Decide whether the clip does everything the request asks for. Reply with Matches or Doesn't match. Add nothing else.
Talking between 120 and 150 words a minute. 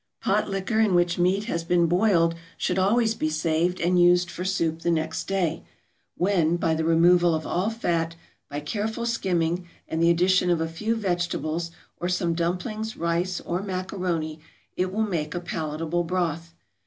Doesn't match